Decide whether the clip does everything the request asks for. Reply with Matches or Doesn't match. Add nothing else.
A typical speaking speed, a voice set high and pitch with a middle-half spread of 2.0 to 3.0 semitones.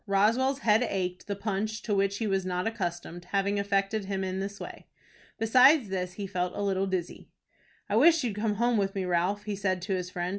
Doesn't match